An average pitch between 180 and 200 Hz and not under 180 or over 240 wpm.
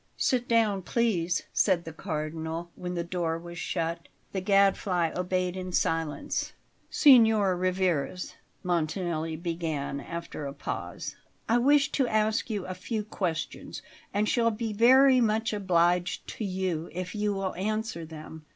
No: medium, 185 Hz; average, 140 wpm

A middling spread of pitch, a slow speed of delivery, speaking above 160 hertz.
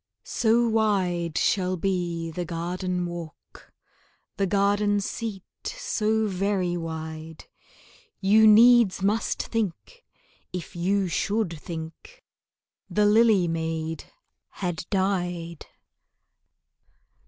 Yes: average, 3.7 semitones; slow, 90 wpm; medium, 185 Hz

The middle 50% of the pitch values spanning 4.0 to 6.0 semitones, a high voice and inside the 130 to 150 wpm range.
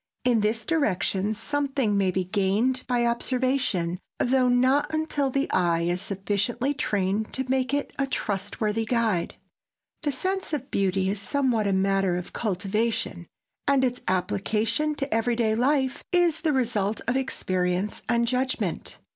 Yes: average, 5.2 semitones; high, 230 Hz; average, 145 wpm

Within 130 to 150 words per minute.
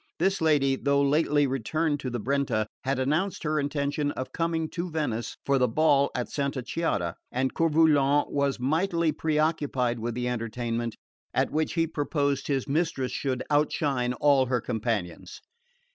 No: average, 160 wpm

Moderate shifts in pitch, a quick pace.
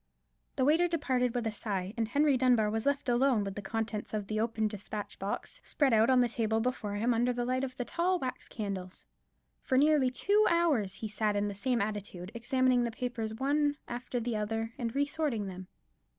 Yes: average, 3.6 semitones; fast, 210 wpm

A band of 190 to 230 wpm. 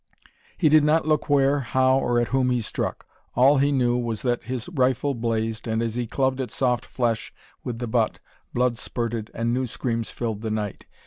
Yes: average, 200 wpm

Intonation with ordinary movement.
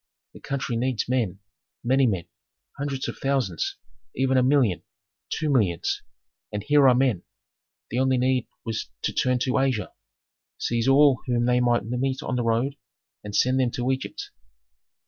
No: narrow, 2.2 semitones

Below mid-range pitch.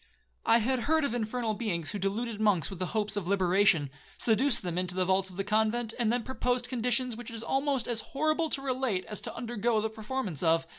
No: high, 220 Hz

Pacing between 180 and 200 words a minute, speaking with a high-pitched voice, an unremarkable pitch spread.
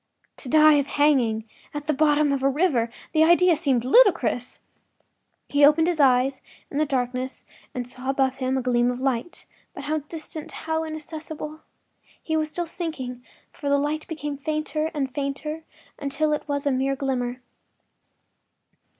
No: average, 165 wpm; very high, 285 Hz; average, 3.0 semitones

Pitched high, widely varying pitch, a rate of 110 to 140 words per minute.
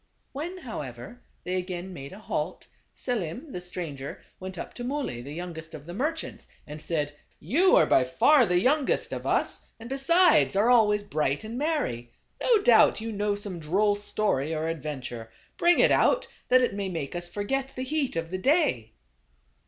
No: high, 200 Hz; wide, 8.4 semitones; average, 185 wpm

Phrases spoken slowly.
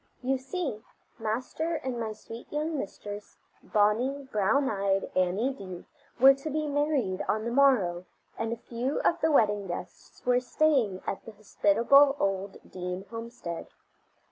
No: average, 145 wpm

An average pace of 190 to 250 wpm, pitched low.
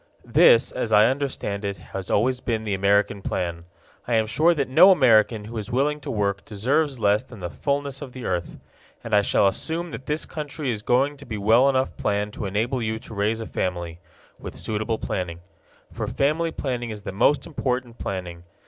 Yes: average, 200 wpm; low, 115 Hz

